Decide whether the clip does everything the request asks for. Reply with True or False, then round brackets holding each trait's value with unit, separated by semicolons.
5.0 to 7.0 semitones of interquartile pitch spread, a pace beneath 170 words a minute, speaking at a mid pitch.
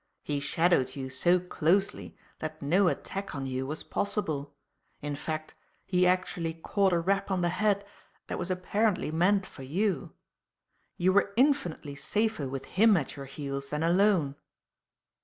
True (5.4 semitones; 155 wpm; 175 Hz)